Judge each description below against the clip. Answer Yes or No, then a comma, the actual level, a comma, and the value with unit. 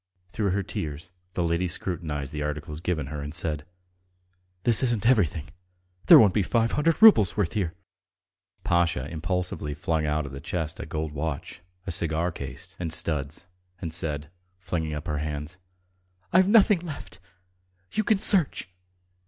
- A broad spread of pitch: No, average, 4.5 semitones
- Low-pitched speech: Yes, very low, 85 Hz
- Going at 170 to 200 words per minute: No, average, 160 wpm